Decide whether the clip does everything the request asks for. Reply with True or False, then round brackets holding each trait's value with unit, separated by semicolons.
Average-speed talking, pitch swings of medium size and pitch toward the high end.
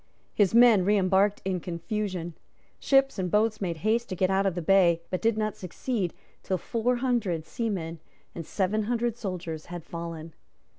True (165 wpm; 4.0 semitones; 195 Hz)